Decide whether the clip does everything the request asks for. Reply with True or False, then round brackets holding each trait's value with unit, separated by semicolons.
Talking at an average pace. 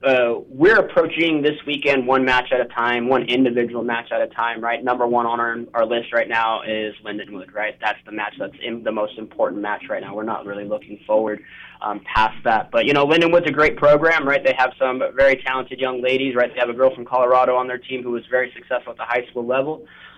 False (240 wpm)